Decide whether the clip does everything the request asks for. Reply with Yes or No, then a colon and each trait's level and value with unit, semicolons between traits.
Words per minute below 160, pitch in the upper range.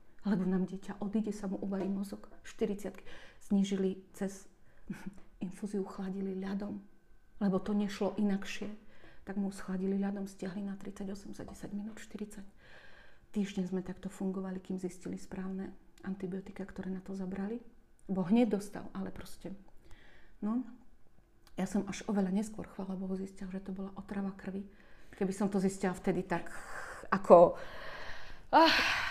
Yes: average, 140 wpm; high, 195 Hz